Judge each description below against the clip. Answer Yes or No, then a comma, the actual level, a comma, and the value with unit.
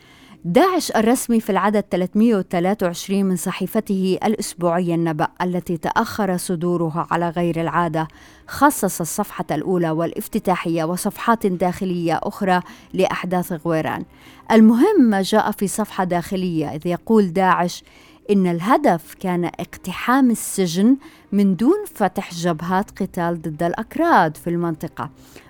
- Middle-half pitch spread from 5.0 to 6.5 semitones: No, average, 3.3 semitones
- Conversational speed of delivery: Yes, average, 110 wpm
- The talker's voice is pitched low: No, medium, 185 Hz